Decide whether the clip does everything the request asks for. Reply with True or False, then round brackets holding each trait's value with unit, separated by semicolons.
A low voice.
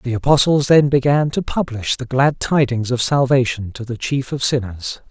True (130 Hz)